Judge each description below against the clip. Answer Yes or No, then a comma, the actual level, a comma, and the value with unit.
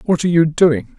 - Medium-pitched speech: Yes, medium, 160 Hz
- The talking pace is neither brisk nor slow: No, fast, 245 wpm